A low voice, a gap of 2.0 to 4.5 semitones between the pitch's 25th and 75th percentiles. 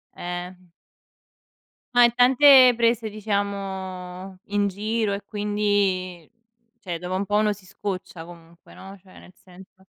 No: high, 200 Hz; narrow, 2.4 semitones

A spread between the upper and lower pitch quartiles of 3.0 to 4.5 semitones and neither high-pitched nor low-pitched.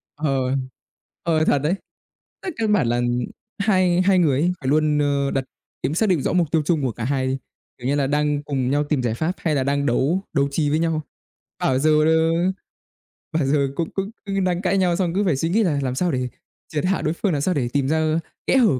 Yes: average, 4.1 semitones; medium, 155 Hz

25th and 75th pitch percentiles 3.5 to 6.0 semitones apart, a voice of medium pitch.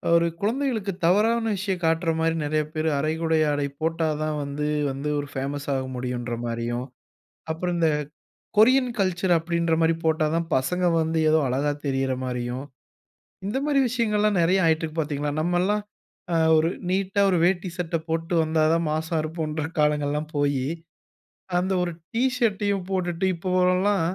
Yes: average, 3.8 semitones; medium, 165 Hz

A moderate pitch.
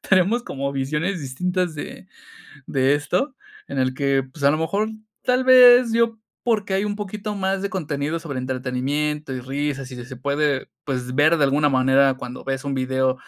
Yes: medium, 145 Hz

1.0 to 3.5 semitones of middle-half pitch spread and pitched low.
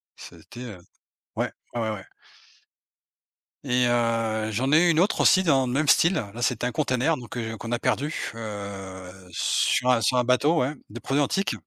No: average, 4.2 semitones; low, 125 Hz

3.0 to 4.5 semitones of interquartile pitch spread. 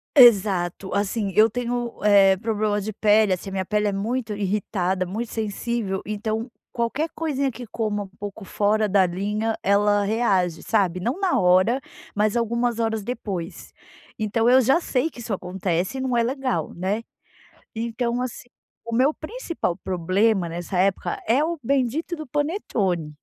Yes: average, 3.7 semitones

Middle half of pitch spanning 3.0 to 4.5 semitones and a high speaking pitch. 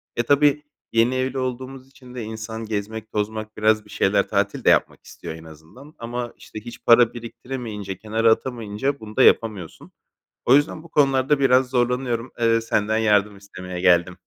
No: average, 3.5 semitones; low, 115 Hz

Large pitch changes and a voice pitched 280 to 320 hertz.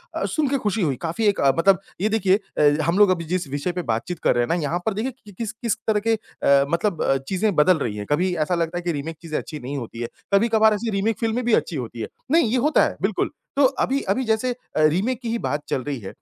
No: wide, 6.6 semitones; medium, 185 Hz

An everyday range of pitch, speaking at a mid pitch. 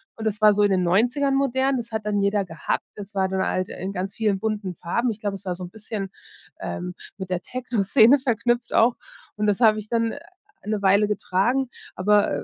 No: average, 3.2 semitones; high, 210 Hz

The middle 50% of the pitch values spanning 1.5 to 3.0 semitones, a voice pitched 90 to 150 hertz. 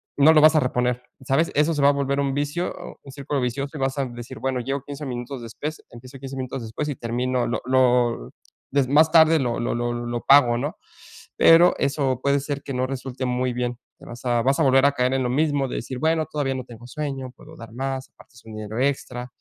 Yes: narrow, 2.4 semitones; low, 135 Hz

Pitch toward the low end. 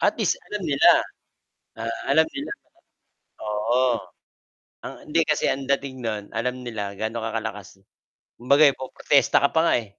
Yes: low, 125 Hz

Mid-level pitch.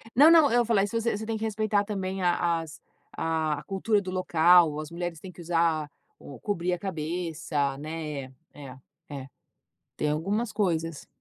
Yes: medium, 175 Hz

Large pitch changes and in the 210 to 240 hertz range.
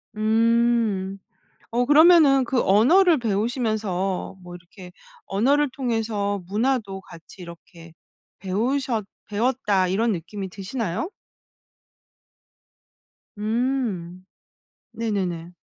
No: average, 4.5 semitones; high, 215 Hz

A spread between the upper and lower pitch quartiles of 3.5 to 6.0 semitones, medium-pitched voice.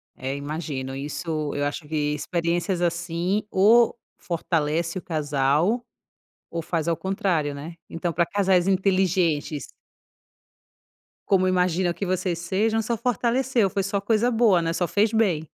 Yes: average, 3.8 semitones; medium, 175 Hz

